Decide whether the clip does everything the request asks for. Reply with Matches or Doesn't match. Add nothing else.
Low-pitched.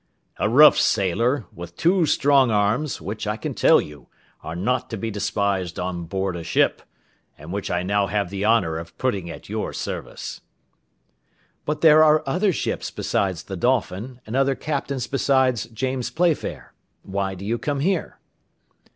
Matches